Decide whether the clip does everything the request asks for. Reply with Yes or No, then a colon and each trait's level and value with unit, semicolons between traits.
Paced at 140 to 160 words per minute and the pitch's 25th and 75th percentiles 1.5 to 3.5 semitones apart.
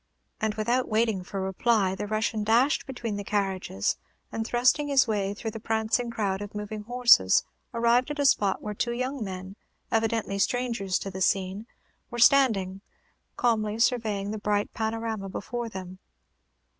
Yes: average, 155 wpm; average, 3.2 semitones